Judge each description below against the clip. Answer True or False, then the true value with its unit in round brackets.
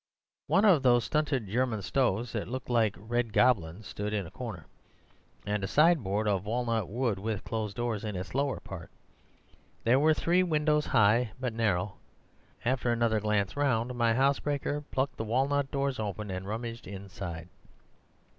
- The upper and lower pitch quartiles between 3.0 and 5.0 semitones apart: True (4.2 semitones)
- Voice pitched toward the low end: True (115 Hz)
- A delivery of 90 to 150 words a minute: False (160 wpm)